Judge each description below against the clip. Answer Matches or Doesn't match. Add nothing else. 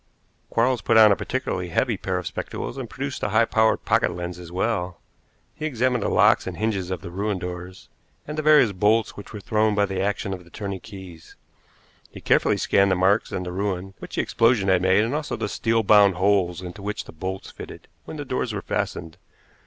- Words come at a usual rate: Doesn't match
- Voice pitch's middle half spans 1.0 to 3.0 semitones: Doesn't match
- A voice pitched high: Doesn't match